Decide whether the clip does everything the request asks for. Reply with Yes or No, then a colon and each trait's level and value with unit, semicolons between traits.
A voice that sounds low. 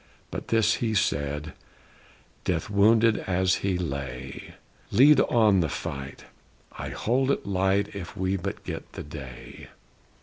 Yes: very low, 95 Hz